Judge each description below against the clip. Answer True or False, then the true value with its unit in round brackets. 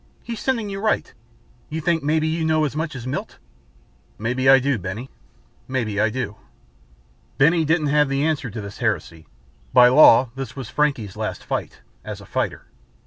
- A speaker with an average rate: True (180 wpm)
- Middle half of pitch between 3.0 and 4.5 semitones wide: False (4.9 semitones)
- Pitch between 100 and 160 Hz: True (135 Hz)